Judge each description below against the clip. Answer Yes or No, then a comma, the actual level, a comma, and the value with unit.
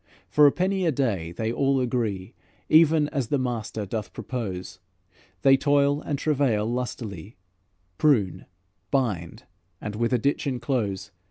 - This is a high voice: No, low, 125 Hz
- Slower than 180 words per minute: Yes, average, 140 wpm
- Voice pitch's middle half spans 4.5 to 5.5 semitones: Yes, average, 5.1 semitones